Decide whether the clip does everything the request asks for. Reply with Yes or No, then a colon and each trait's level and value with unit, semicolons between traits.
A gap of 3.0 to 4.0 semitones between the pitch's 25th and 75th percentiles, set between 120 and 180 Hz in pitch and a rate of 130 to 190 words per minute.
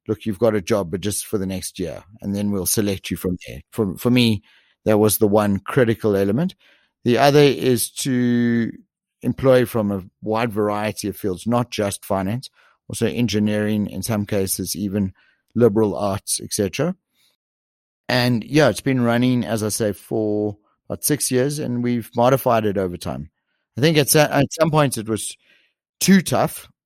No: average, 3.4 semitones; low, 110 Hz; average, 175 wpm